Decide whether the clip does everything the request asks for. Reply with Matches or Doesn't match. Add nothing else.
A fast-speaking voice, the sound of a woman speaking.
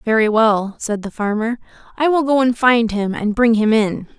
Matches